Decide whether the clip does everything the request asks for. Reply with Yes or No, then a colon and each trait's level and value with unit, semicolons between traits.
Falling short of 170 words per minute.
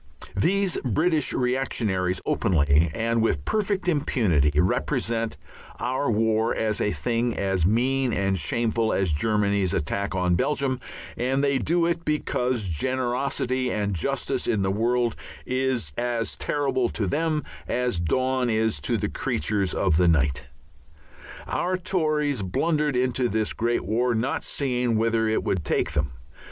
Yes: average, 140 wpm